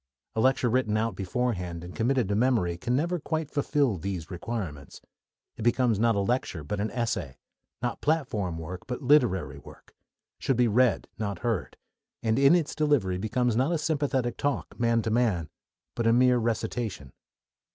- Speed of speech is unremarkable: Yes, average, 170 wpm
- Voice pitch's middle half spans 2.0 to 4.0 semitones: No, average, 4.9 semitones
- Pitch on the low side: Yes, low, 115 Hz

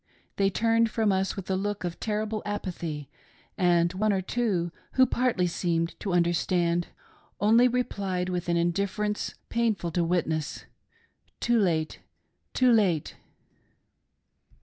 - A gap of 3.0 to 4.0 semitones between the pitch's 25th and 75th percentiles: Yes, average, 3.7 semitones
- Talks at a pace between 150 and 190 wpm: No, average, 140 wpm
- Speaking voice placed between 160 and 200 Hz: Yes, high, 190 Hz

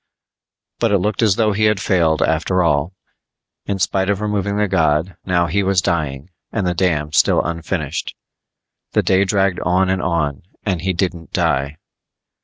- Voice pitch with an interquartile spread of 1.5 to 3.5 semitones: Yes, average, 3.1 semitones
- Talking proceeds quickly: No, average, 170 wpm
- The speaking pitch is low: Yes, very low, 90 Hz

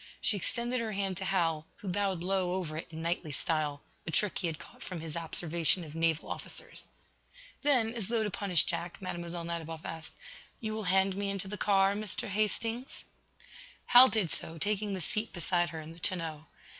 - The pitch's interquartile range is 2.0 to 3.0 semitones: No, average, 3.9 semitones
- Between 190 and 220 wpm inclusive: Yes, average, 195 wpm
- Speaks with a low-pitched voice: No, medium, 185 Hz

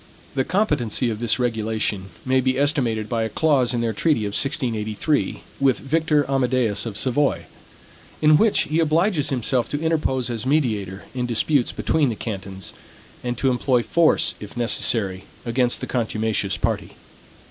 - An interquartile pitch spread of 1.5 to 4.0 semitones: No, average, 4.4 semitones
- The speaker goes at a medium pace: Yes, average, 155 wpm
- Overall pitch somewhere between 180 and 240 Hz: No, low, 125 Hz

